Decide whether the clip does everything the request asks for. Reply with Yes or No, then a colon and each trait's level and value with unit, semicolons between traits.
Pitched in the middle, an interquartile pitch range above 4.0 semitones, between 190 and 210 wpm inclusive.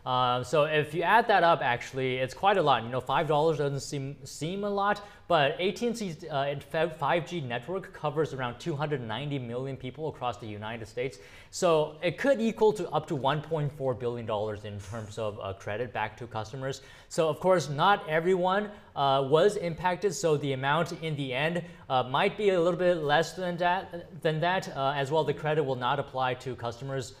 Yes: medium, 150 Hz; average, 5.0 semitones; average, 195 wpm